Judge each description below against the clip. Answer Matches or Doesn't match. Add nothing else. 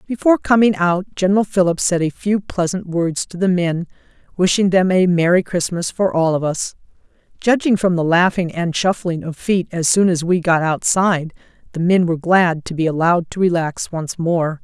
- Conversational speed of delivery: Matches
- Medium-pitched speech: Matches